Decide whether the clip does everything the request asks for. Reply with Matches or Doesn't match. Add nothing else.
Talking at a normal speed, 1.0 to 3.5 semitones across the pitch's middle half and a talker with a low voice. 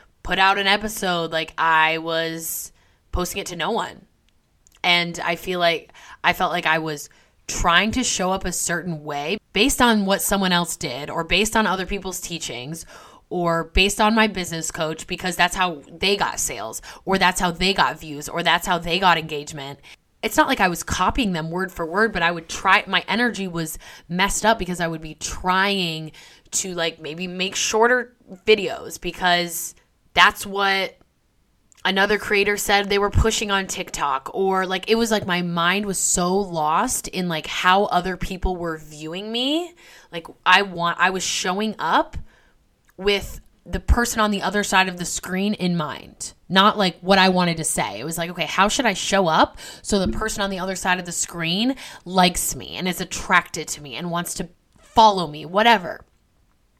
Doesn't match